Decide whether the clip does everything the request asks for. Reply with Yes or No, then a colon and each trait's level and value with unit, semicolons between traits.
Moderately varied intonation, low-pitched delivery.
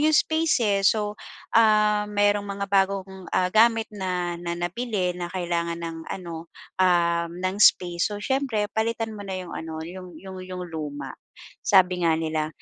No: average, 3.3 semitones; medium, 185 Hz